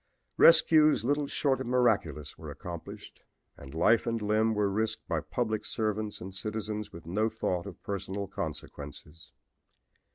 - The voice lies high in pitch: No, low, 105 Hz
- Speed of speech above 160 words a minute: No, average, 140 wpm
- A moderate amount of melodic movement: Yes, average, 3.9 semitones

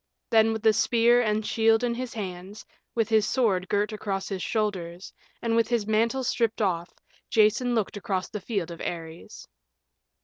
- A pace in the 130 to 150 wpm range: No, average, 170 wpm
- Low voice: No, high, 215 Hz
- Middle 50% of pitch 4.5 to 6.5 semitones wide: No, average, 3.0 semitones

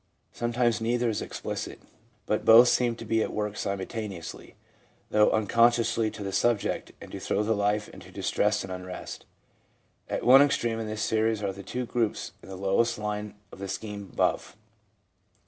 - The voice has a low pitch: Yes, low, 110 Hz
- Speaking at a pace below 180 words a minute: Yes, average, 165 wpm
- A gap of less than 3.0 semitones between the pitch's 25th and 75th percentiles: Yes, narrow, 2.4 semitones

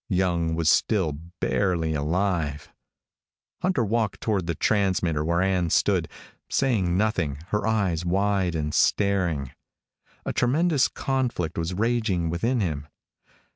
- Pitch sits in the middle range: No, very low, 90 Hz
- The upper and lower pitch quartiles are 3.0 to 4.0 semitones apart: No, average, 4.6 semitones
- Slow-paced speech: Yes, slow, 120 wpm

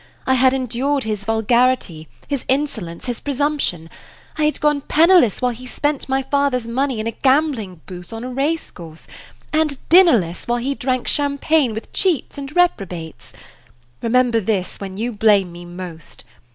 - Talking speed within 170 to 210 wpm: No, average, 160 wpm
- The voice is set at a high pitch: Yes, very high, 250 Hz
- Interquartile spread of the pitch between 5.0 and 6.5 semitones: Yes, wide, 5.5 semitones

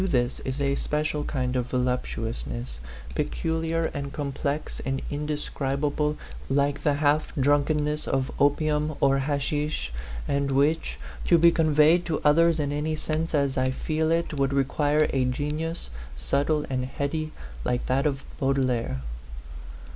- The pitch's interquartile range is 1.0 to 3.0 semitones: Yes, narrow, 2.4 semitones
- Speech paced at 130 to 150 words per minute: Yes, average, 140 wpm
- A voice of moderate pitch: Yes, medium, 145 Hz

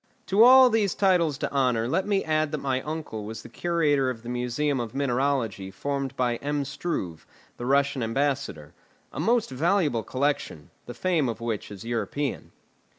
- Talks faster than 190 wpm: No, average, 170 wpm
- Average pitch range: Yes, average, 4.7 semitones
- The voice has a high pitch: No, medium, 140 Hz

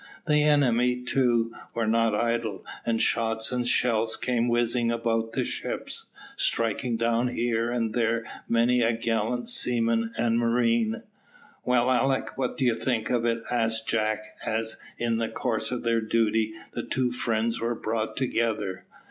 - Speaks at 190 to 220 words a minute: No, average, 155 wpm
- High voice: No, low, 115 Hz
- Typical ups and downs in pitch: No, narrow, 1.3 semitones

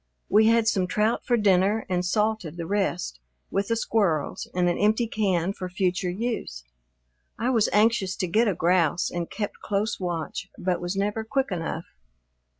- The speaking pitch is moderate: No, high, 195 Hz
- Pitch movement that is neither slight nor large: Yes, average, 3.6 semitones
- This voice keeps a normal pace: Yes, average, 170 wpm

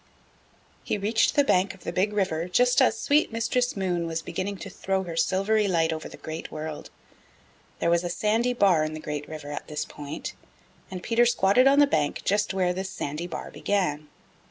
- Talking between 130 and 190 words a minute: No, average, 200 wpm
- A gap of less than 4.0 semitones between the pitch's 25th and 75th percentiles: No, average, 4.7 semitones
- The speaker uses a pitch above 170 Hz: Yes, medium, 185 Hz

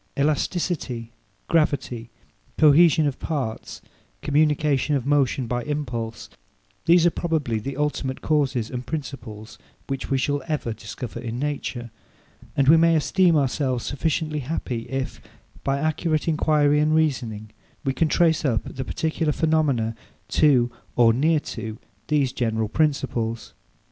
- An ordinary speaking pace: No, slow, 130 wpm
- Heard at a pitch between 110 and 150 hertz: Yes, medium, 140 Hz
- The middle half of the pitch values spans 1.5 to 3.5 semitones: No, average, 4.2 semitones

